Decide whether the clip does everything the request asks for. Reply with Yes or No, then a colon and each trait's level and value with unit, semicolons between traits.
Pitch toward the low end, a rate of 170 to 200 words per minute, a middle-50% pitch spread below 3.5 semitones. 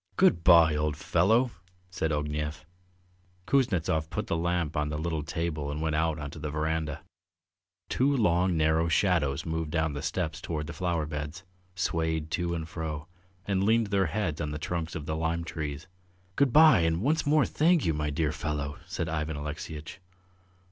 Yes: very low, 80 Hz; average, 175 wpm; narrow, 2.4 semitones